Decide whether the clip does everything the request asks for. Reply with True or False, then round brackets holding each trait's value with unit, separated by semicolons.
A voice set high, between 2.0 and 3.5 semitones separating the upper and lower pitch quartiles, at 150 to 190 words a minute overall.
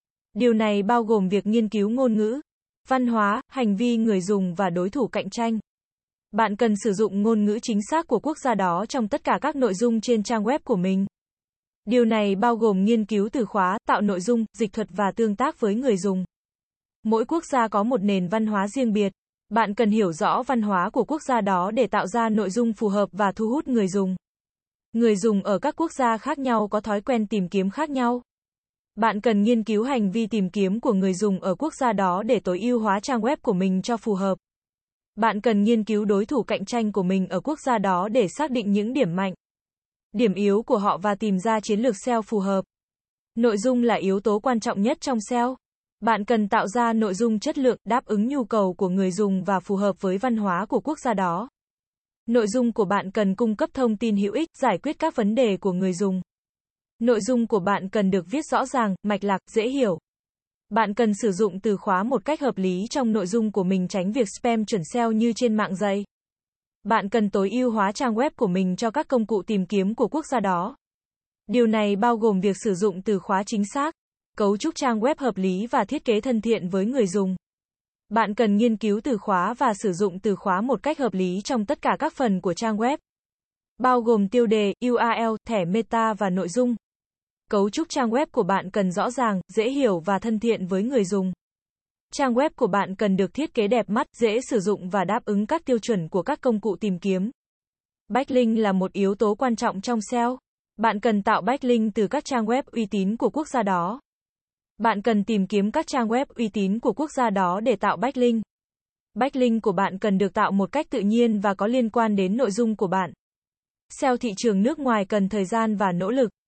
False (220 Hz; 3.2 semitones; 230 wpm)